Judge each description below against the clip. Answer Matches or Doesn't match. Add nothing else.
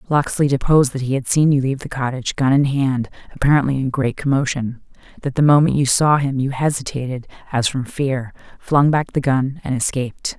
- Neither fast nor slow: Matches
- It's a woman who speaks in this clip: Matches